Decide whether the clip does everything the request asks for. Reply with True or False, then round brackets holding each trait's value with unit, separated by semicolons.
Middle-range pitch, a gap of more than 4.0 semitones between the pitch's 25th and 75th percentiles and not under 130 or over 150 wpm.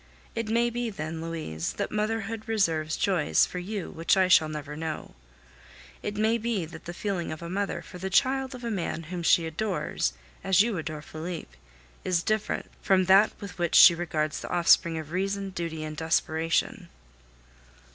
False (180 Hz; 4.5 semitones; 175 wpm)